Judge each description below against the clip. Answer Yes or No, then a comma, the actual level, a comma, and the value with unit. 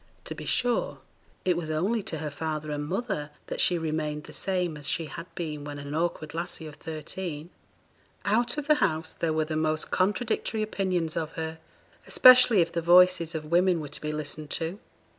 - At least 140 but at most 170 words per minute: No, average, 195 wpm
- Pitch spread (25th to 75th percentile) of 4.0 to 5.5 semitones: No, average, 3.1 semitones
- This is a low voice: No, medium, 165 Hz